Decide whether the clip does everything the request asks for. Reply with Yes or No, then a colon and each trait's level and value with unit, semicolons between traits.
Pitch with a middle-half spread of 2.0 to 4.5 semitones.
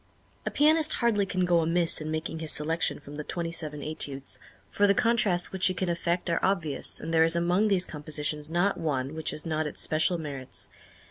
Yes: average, 3.2 semitones